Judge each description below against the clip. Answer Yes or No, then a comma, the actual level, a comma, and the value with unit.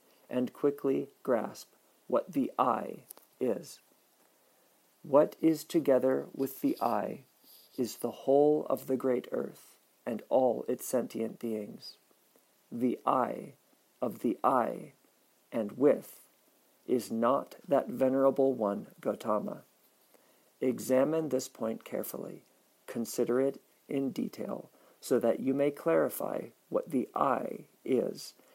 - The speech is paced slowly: Yes, slow, 115 wpm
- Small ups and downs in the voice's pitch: Yes, narrow, 1.8 semitones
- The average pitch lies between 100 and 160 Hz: Yes, low, 135 Hz